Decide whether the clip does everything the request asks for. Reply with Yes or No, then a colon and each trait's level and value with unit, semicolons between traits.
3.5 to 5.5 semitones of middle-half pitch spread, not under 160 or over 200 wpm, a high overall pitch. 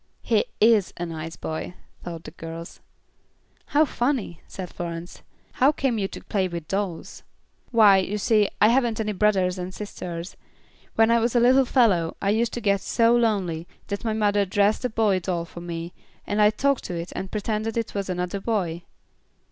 Yes: average, 4.2 semitones; average, 185 wpm; high, 200 Hz